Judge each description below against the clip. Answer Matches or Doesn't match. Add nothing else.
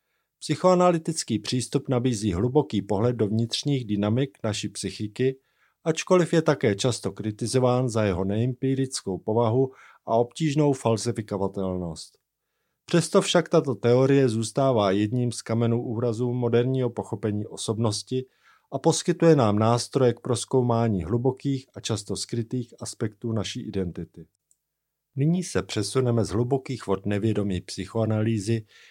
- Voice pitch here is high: Doesn't match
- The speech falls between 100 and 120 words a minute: Matches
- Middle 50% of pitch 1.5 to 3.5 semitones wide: Doesn't match